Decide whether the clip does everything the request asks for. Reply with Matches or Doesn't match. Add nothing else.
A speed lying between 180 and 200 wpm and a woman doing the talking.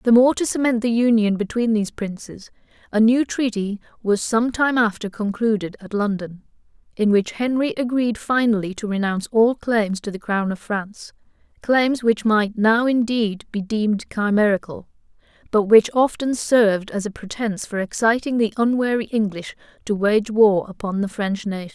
Doesn't match